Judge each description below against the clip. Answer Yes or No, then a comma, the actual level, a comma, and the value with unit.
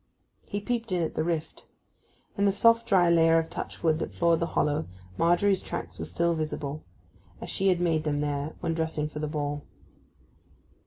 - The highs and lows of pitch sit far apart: No, average, 2.9 semitones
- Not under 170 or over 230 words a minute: Yes, average, 190 wpm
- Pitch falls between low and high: Yes, medium, 165 Hz